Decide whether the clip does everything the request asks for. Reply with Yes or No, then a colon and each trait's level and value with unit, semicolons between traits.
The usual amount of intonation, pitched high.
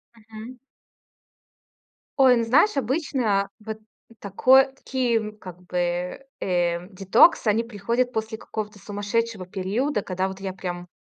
Yes: average, 4.1 semitones; high, 215 Hz